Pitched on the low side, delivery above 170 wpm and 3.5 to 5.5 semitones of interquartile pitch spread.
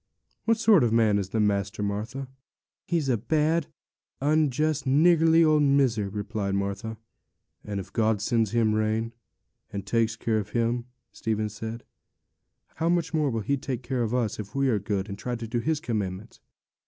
Yes: low, 115 Hz; average, 180 wpm; average, 4.8 semitones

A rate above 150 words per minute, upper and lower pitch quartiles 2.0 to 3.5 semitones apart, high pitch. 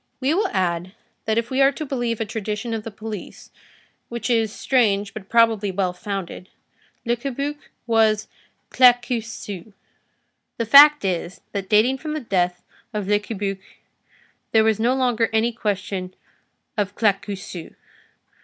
No: average, 145 wpm; average, 3.2 semitones; high, 220 Hz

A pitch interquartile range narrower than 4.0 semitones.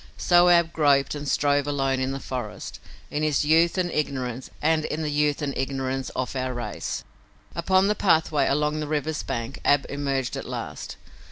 Yes: average, 2.7 semitones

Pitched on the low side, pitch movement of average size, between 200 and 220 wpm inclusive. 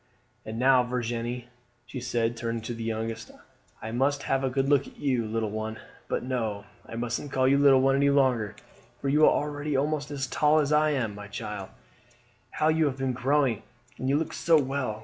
Yes: low, 130 Hz; average, 3.6 semitones; fast, 205 wpm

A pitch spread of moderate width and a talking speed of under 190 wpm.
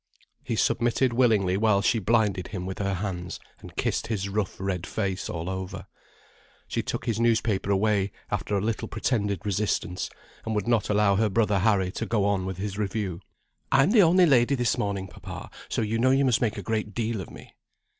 No: average, 3.0 semitones; average, 195 wpm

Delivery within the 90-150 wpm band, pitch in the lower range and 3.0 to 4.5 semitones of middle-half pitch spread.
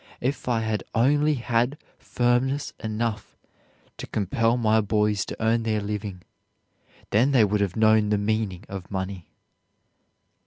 No: average, 140 wpm; low, 110 Hz; narrow, 2.6 semitones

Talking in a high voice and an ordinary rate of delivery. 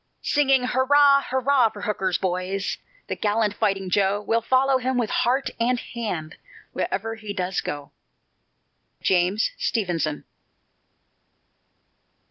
No: high, 215 Hz; slow, 110 wpm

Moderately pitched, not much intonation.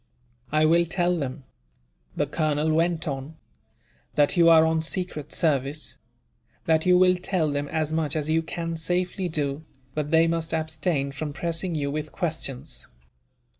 Yes: medium, 160 Hz; narrow, 2.2 semitones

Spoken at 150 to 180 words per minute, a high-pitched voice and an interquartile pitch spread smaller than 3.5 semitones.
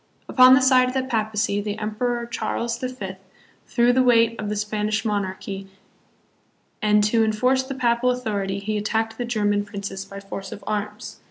Yes: average, 175 wpm; high, 215 Hz; average, 2.9 semitones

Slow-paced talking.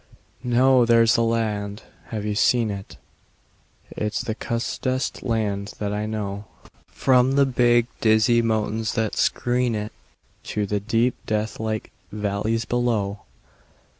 Yes: slow, 125 wpm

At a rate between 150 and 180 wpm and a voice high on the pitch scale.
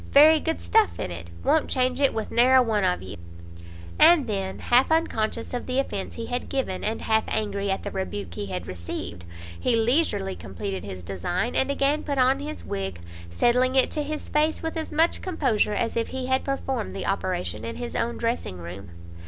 No: average, 200 wpm; high, 230 Hz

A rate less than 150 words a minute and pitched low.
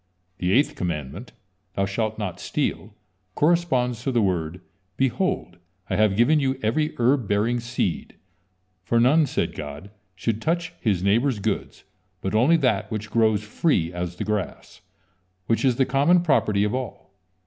No: average, 155 wpm; low, 110 Hz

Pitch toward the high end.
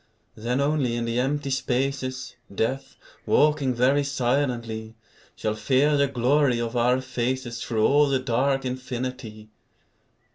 No: low, 130 Hz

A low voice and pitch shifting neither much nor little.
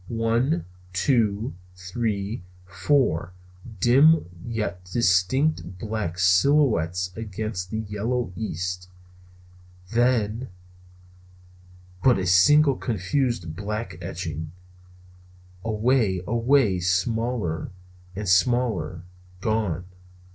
Yes: low, 105 Hz; average, 4.8 semitones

